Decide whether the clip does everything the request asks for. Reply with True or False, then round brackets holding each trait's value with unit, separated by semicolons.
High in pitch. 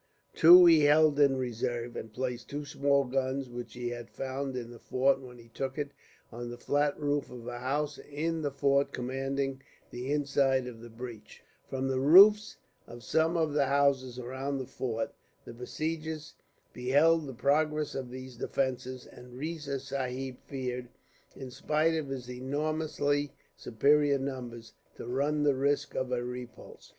False (135 Hz)